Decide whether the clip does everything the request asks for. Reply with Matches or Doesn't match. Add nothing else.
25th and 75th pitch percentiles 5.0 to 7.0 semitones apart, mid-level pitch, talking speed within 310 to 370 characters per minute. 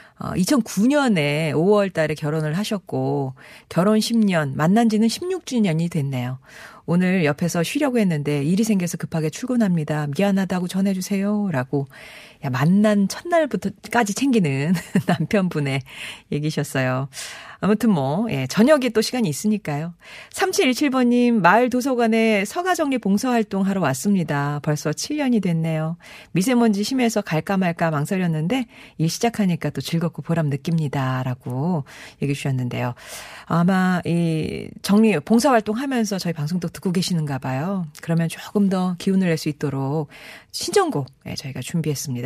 Matches